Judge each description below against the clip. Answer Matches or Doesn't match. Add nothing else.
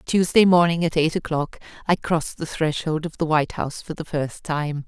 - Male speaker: Doesn't match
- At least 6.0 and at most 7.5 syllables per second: Doesn't match